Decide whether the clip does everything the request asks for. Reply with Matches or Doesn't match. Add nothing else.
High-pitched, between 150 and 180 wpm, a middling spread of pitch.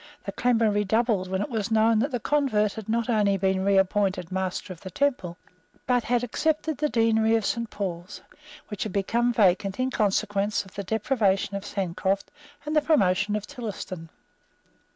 Matches